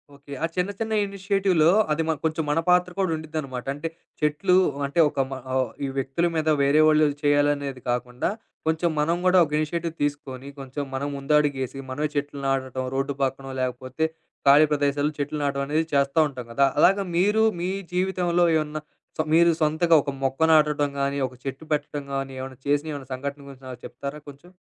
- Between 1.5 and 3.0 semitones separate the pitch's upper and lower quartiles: Yes, average, 2.7 semitones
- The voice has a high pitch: No, medium, 145 Hz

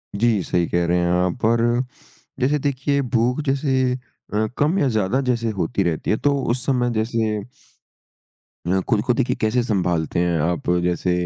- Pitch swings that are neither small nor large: No, wide, 6.1 semitones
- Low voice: Yes, low, 115 Hz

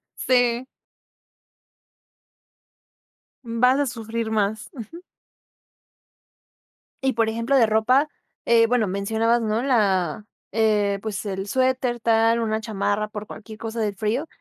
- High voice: Yes, high, 225 Hz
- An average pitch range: No, narrow, 2.1 semitones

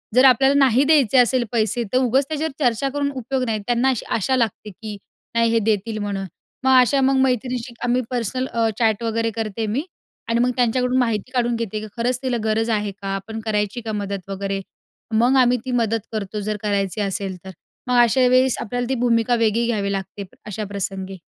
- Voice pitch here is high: Yes, high, 230 Hz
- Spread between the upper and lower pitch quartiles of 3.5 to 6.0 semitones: No, average, 3.1 semitones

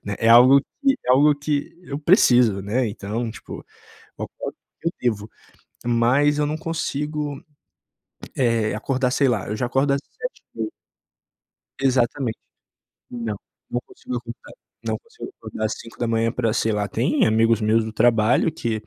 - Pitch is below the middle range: Yes, low, 120 Hz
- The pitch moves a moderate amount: Yes, average, 4.1 semitones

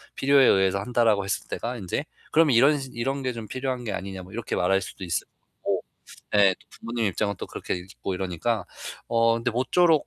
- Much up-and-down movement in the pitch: No, average, 4.7 semitones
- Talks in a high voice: No, low, 115 Hz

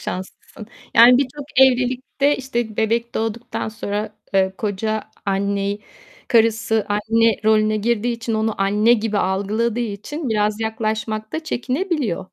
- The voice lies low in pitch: No, high, 220 Hz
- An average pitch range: No, narrow, 2.3 semitones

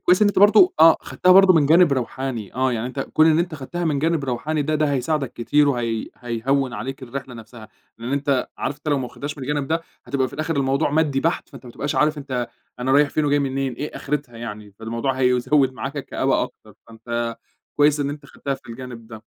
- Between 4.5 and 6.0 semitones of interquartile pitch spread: No, average, 3.3 semitones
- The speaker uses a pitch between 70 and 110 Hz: No, low, 135 Hz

